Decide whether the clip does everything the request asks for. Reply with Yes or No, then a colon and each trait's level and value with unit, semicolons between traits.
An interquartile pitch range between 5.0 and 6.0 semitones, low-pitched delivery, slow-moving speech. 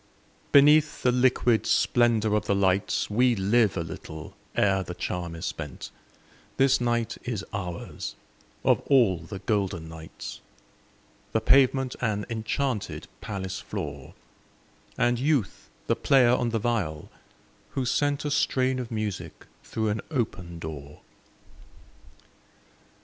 Yes: average, 5.3 semitones; low, 110 Hz; slow, 125 wpm